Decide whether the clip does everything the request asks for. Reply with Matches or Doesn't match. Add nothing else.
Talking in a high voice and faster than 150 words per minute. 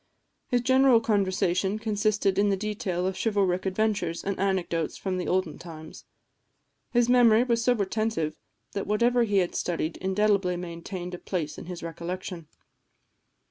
Doesn't match